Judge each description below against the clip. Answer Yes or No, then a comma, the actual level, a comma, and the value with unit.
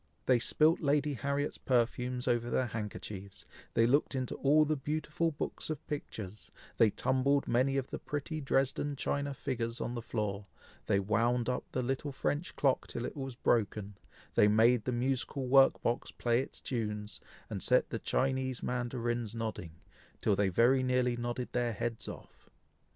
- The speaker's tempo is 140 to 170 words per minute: Yes, average, 165 wpm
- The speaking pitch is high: No, low, 125 Hz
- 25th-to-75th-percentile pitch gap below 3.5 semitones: Yes, average, 2.9 semitones